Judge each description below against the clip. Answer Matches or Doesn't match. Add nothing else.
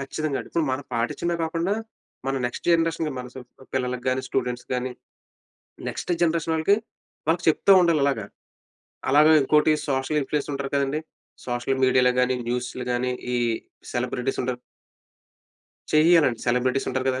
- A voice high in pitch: Doesn't match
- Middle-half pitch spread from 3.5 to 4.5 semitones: Matches